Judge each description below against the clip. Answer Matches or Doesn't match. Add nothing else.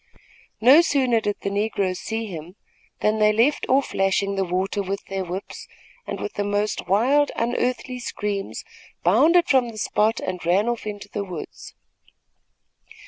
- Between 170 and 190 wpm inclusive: Doesn't match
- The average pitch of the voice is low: Doesn't match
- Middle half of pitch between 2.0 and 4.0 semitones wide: Matches